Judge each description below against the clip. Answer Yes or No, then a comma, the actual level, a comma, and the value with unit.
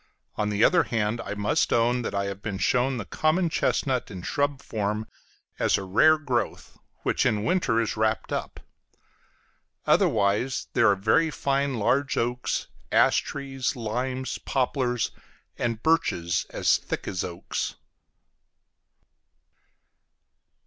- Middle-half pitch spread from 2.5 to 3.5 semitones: No, average, 4.4 semitones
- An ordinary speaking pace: No, slow, 130 wpm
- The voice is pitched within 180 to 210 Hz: No, low, 120 Hz